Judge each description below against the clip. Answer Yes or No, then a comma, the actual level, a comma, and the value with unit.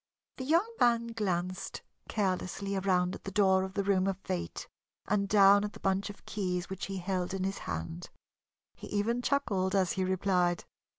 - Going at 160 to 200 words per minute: Yes, average, 180 wpm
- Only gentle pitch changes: Yes, narrow, 1.7 semitones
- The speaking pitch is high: Yes, high, 195 Hz